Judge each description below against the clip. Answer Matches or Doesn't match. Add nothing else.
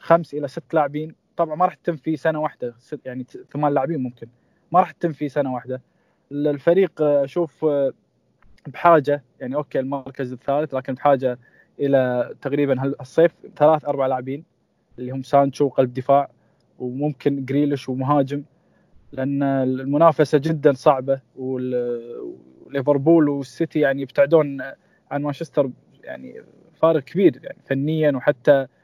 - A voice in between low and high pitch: Matches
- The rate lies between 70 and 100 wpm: Doesn't match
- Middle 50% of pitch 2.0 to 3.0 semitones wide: Matches